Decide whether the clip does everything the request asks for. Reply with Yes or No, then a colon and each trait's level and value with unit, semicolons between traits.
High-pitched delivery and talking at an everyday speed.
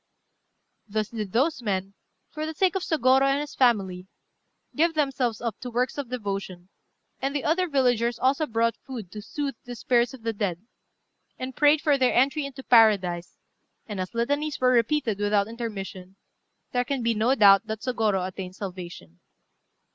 Yes: high, 235 Hz; average, 170 wpm